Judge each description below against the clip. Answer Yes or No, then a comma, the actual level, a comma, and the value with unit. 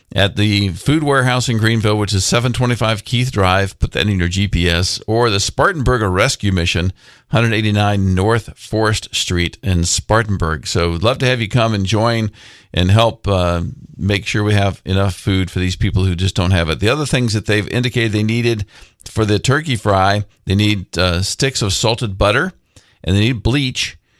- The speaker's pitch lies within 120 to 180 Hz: No, low, 105 Hz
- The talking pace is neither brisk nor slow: Yes, average, 190 wpm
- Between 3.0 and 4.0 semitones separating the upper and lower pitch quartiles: Yes, average, 3.5 semitones